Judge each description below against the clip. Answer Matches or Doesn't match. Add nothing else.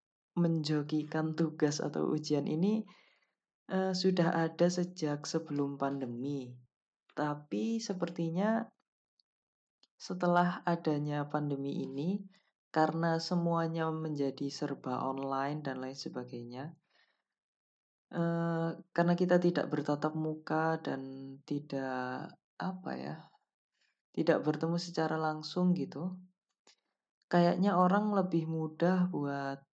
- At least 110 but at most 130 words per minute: Doesn't match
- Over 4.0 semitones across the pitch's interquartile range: Doesn't match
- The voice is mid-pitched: Matches